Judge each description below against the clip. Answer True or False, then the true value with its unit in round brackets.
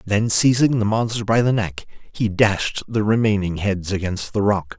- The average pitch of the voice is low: True (105 Hz)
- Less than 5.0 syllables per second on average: True (4.5 syllables/s)